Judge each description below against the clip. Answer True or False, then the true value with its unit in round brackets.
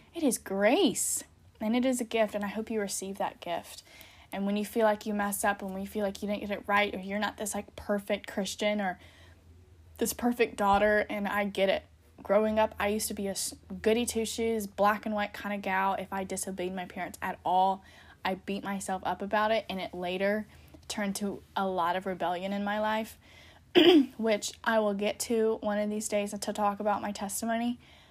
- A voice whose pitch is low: False (205 Hz)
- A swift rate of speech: True (220 wpm)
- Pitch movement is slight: True (1.9 semitones)